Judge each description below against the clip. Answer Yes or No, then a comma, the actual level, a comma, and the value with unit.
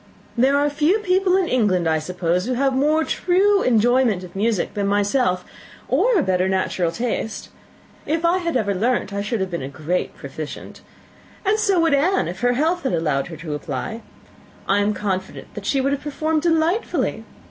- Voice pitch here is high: Yes, high, 235 Hz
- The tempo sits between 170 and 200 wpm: Yes, average, 190 wpm